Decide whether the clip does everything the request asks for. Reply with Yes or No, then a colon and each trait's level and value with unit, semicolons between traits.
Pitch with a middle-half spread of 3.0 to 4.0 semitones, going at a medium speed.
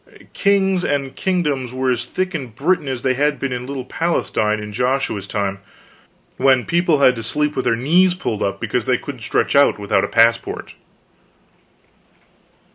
No: wide, 5.6 semitones; average, 170 wpm